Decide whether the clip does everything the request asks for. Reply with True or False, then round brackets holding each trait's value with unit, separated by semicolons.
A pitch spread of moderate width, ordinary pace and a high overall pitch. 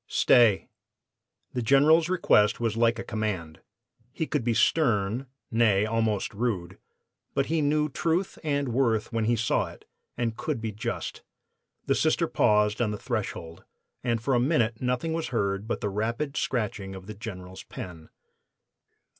False (3.9 semitones; 155 wpm; 115 Hz)